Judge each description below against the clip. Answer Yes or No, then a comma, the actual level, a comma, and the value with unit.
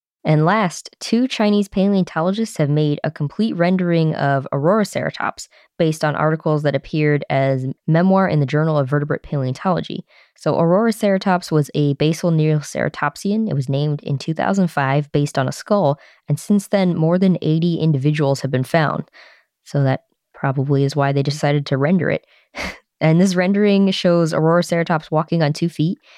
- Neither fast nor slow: Yes, average, 165 wpm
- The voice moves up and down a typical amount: Yes, average, 4.0 semitones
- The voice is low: No, medium, 160 Hz